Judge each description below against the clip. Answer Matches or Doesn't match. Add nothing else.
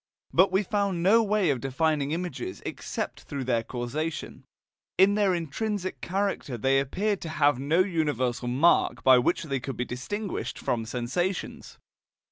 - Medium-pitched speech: Matches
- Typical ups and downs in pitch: Doesn't match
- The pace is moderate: Matches